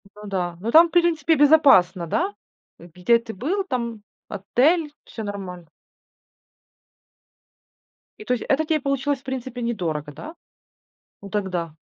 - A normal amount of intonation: No, wide, 7.7 semitones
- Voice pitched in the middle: No, high, 235 Hz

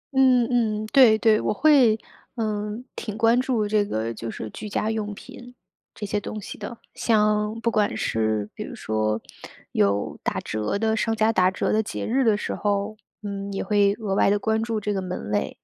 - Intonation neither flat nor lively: No, narrow, 2.2 semitones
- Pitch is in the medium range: No, high, 210 Hz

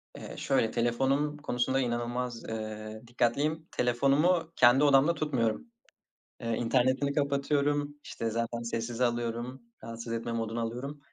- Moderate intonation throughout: Yes, average, 3.4 semitones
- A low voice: Yes, low, 125 Hz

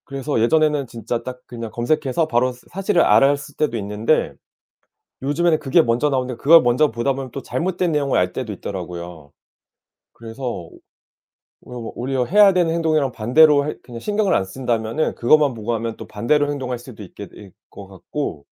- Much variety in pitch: No, average, 4.8 semitones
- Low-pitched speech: Yes, low, 130 Hz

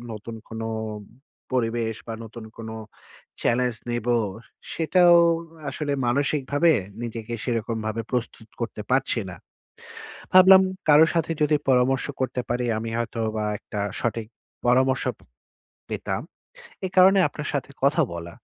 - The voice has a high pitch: No, low, 120 Hz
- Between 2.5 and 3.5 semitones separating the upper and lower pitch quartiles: No, average, 4.1 semitones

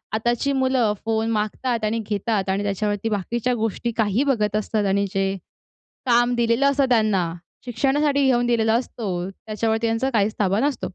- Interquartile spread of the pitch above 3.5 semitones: No, average, 2.7 semitones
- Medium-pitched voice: No, high, 225 Hz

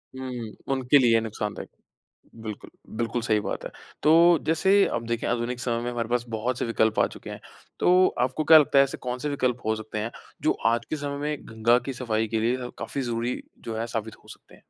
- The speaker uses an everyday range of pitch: No, narrow, 2.3 semitones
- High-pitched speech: No, low, 120 Hz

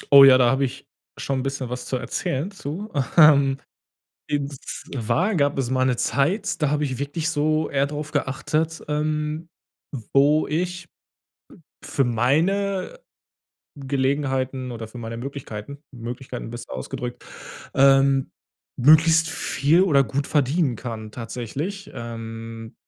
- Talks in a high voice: No, medium, 140 Hz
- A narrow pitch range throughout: No, average, 3.5 semitones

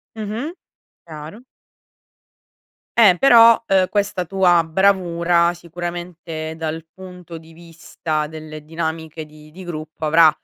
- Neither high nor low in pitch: Yes, medium, 170 Hz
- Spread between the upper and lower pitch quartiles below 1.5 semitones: No, average, 2.7 semitones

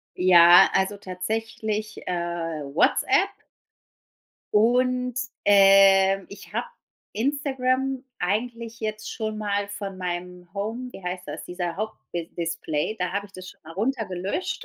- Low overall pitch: No, high, 200 Hz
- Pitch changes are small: No, average, 3.7 semitones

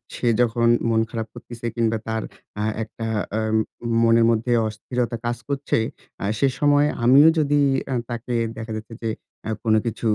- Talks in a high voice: No, low, 115 Hz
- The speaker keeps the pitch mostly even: Yes, narrow, 1.9 semitones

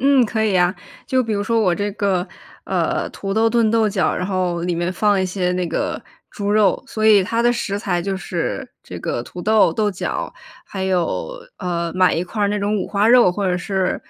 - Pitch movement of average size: Yes, average, 3.1 semitones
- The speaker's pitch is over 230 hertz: No, high, 200 Hz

